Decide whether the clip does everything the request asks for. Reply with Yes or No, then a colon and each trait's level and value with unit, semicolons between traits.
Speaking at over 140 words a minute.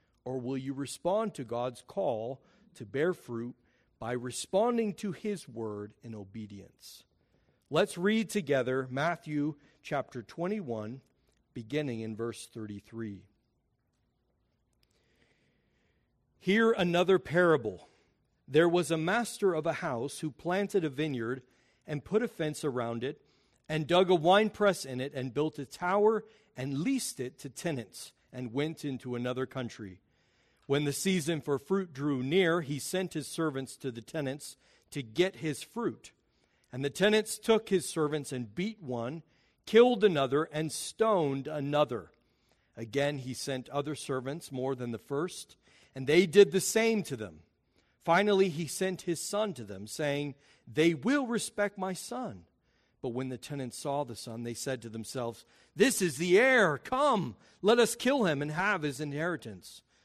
Yes: average, 150 wpm